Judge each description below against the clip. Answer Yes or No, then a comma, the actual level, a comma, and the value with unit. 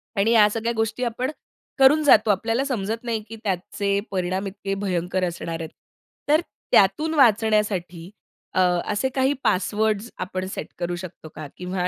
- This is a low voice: No, high, 205 Hz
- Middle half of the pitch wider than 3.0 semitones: Yes, average, 3.8 semitones